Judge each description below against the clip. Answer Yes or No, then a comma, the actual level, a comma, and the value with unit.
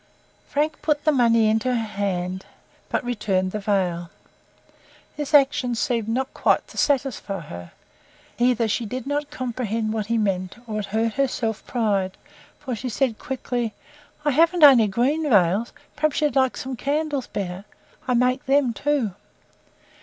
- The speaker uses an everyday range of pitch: Yes, average, 4.6 semitones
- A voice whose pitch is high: Yes, high, 235 Hz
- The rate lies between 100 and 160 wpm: Yes, average, 155 wpm